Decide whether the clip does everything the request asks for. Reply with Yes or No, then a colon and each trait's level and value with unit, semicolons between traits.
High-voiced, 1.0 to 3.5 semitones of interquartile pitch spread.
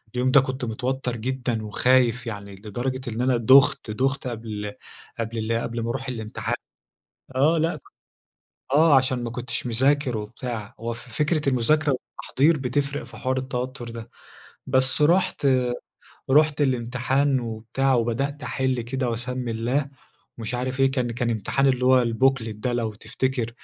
No: low, 125 Hz; narrow, 2.5 semitones